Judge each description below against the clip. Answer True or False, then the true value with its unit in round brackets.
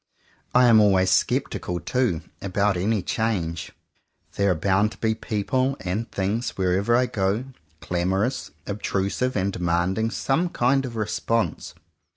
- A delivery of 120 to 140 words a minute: True (135 wpm)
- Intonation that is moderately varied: True (3.8 semitones)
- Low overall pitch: True (105 Hz)